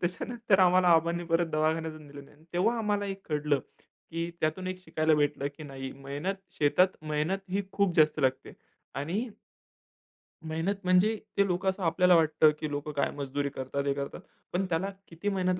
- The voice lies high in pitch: No, medium, 165 Hz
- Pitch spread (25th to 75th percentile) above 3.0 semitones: Yes, average, 3.8 semitones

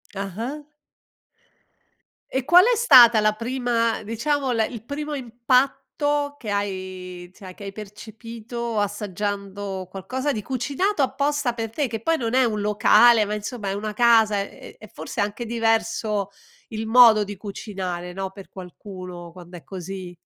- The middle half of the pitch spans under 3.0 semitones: No, average, 3.7 semitones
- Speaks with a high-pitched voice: Yes, high, 220 Hz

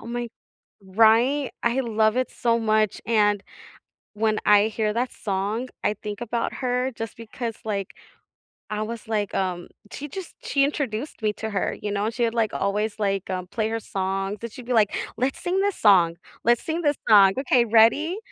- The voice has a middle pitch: No, high, 220 Hz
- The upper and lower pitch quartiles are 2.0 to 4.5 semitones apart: Yes, average, 2.7 semitones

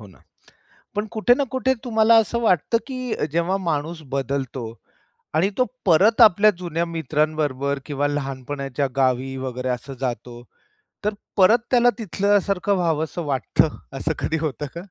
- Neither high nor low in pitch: Yes, medium, 160 Hz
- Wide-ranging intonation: Yes, wide, 6.9 semitones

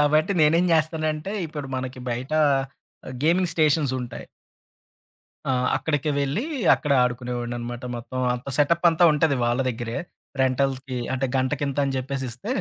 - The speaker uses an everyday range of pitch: Yes, average, 3.6 semitones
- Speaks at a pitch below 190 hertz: Yes, medium, 140 Hz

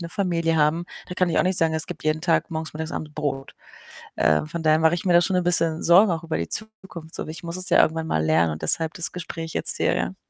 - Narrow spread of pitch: Yes, narrow, 2.0 semitones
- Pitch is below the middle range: No, medium, 165 Hz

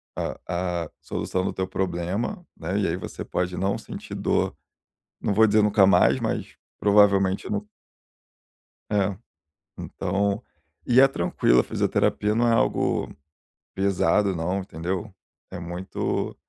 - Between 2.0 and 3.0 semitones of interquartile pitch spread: Yes, narrow, 2.4 semitones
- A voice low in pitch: Yes, very low, 95 Hz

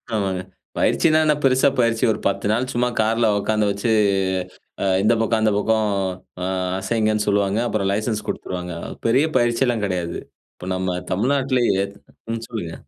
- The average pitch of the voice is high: No, low, 110 Hz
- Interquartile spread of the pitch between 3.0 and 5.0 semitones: Yes, average, 3.3 semitones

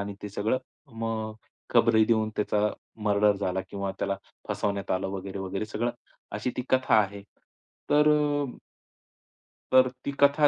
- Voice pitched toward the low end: Yes, low, 105 Hz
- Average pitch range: Yes, average, 4.1 semitones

